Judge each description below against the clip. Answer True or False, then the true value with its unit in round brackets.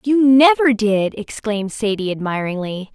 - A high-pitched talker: True (220 Hz)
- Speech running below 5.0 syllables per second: True (4.6 syllables/s)